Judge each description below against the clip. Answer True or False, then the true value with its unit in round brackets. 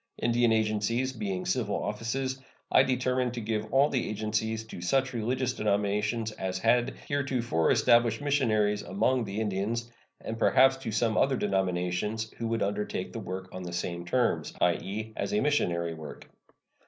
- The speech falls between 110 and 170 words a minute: True (155 wpm)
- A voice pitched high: False (110 Hz)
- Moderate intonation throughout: True (3.7 semitones)